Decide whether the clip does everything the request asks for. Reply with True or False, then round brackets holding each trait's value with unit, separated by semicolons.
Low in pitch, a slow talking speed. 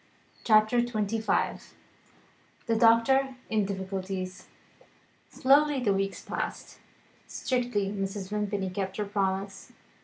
False (205 Hz; 95 wpm)